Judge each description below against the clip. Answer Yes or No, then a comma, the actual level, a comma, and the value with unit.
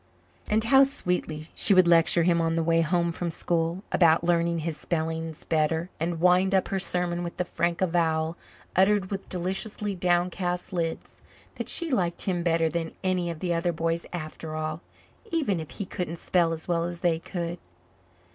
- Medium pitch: Yes, medium, 170 Hz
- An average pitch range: No, narrow, 1.8 semitones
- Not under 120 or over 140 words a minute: No, average, 180 wpm